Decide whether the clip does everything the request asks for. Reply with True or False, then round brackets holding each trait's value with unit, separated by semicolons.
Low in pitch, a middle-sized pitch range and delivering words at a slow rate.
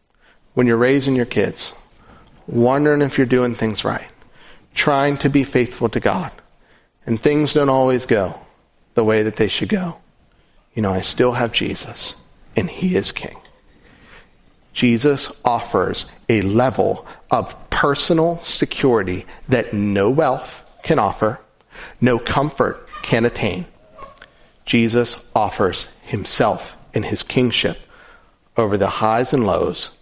True (125 Hz; 3.4 semitones; 130 wpm)